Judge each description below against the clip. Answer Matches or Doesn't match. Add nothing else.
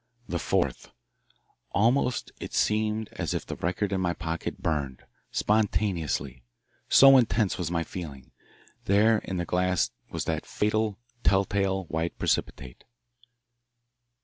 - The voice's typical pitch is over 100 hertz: Doesn't match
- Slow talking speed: Matches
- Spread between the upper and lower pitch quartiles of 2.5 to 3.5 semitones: Doesn't match